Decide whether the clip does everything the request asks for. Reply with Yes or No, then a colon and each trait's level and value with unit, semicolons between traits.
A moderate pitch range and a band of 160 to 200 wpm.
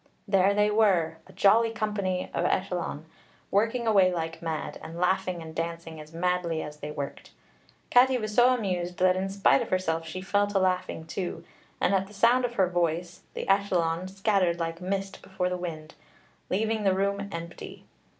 Yes: average, 3.1 semitones; average, 175 wpm